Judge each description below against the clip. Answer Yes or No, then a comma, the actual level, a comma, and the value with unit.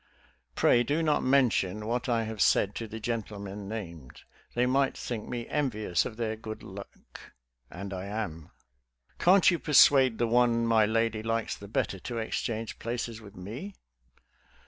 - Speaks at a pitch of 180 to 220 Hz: No, low, 115 Hz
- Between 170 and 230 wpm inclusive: No, average, 160 wpm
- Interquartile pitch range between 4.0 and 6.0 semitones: No, average, 2.7 semitones